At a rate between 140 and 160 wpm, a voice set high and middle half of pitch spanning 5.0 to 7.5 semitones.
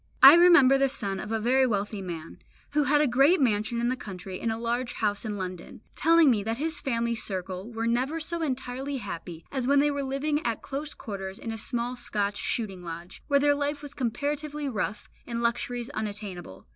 No: fast, 205 wpm; high, 240 Hz; average, 5.3 semitones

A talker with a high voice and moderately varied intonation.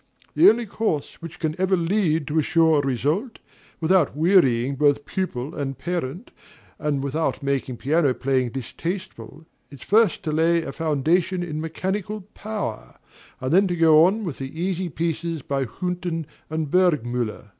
No: medium, 160 Hz; average, 4.5 semitones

